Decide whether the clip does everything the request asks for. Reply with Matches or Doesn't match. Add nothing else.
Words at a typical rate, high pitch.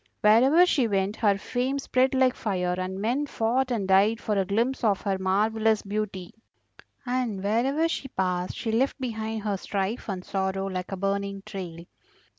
Matches